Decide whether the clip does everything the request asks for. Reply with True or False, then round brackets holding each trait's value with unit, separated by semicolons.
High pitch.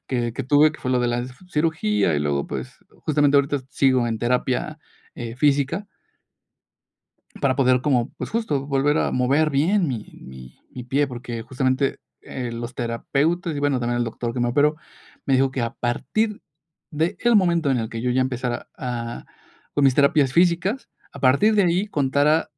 False (135 Hz)